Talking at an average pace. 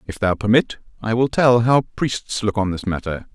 No: fast, 215 wpm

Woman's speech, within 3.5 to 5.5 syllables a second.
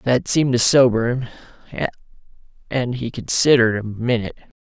No: male; 5.3 syllables/s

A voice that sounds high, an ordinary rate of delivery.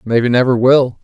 No: low, 125 Hz; average, 175 wpm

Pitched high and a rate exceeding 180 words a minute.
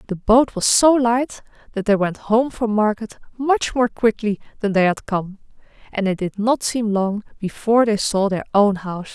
Yes: high, 215 Hz; average, 195 wpm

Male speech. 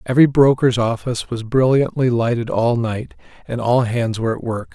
Yes: male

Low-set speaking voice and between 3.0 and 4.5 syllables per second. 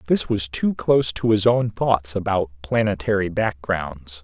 Yes: low, 100 Hz; 4.3 syllables/s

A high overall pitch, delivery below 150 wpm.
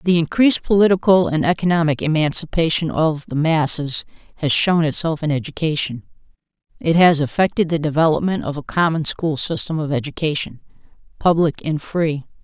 No: medium, 160 Hz; average, 140 wpm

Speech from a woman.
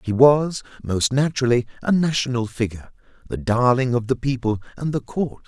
No: male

